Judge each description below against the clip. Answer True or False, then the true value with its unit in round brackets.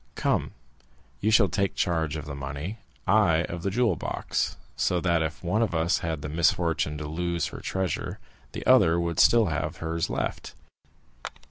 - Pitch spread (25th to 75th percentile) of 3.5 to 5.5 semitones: False (2.7 semitones)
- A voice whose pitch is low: True (85 Hz)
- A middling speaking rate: True (170 wpm)